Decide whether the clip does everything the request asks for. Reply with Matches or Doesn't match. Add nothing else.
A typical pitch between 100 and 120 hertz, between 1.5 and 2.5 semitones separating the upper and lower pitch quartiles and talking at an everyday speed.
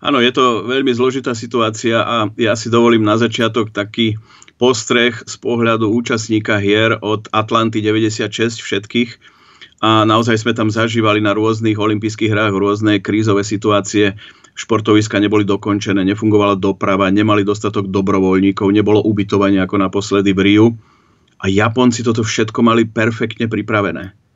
Matches